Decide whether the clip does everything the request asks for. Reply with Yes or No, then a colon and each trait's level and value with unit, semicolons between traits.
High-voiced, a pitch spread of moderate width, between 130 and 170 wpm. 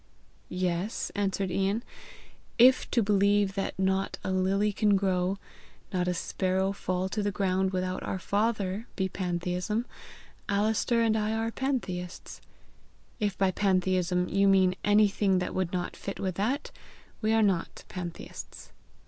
No: high, 195 Hz; narrow, 2.2 semitones; average, 140 wpm